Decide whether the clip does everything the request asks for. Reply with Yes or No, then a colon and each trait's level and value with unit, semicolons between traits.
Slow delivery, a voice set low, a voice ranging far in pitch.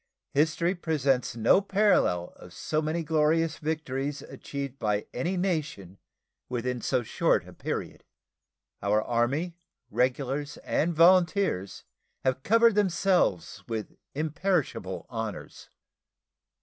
No: slow, 105 wpm; medium, 145 Hz; wide, 6.2 semitones